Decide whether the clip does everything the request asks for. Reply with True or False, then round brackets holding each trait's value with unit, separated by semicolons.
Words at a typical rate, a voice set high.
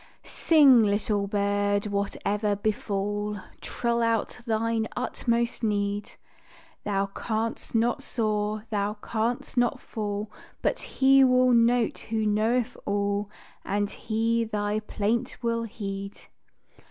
False (110 wpm; 215 Hz)